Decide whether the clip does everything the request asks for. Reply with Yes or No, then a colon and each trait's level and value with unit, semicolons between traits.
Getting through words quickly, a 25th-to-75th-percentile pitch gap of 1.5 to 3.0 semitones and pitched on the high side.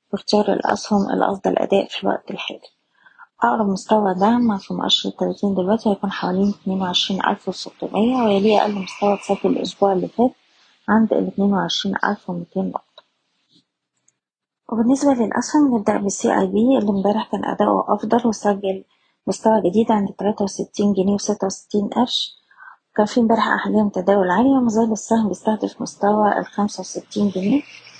Yes: fast, 140 wpm; narrow, 2.4 semitones; high, 205 Hz